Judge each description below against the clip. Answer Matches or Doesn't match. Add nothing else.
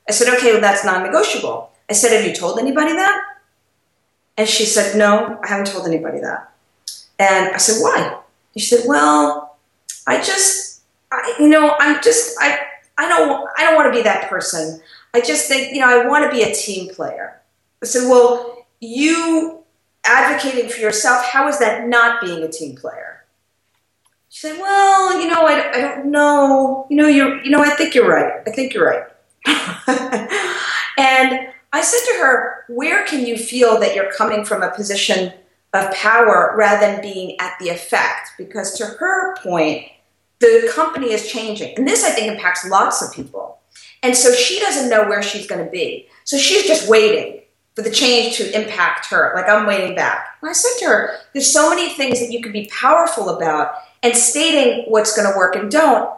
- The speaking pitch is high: Matches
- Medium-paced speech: Matches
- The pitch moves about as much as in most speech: Doesn't match